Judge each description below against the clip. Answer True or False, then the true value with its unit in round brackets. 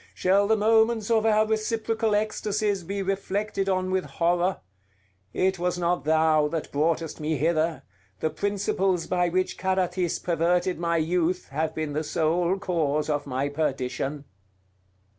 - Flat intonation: False (3.8 semitones)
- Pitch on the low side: False (180 Hz)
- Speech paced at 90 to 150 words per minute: True (140 wpm)